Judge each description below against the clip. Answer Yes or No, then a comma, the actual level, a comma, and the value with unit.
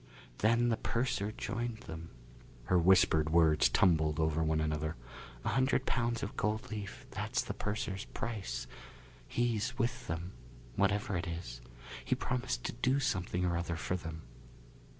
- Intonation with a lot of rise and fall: Yes, wide, 6.0 semitones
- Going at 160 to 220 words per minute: No, average, 150 wpm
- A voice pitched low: Yes, very low, 95 Hz